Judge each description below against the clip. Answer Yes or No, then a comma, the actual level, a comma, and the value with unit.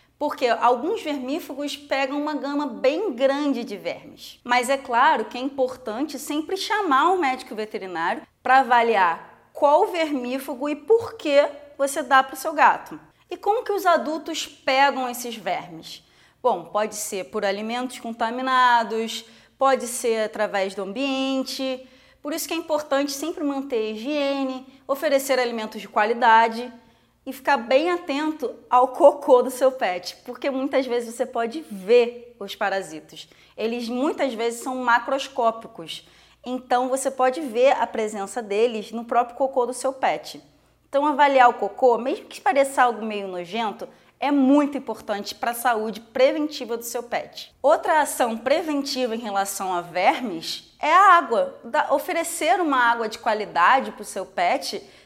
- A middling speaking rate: Yes, average, 155 wpm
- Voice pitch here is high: Yes, very high, 260 Hz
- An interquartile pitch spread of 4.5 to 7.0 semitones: No, average, 4.0 semitones